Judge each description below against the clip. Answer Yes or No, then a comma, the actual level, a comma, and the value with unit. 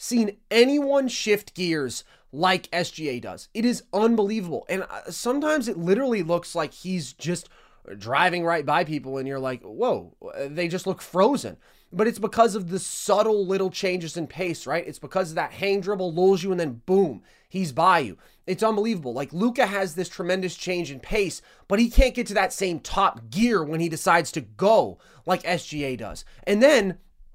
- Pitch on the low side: No, medium, 185 Hz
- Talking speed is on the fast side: No, average, 185 wpm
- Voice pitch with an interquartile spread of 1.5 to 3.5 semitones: No, average, 4.2 semitones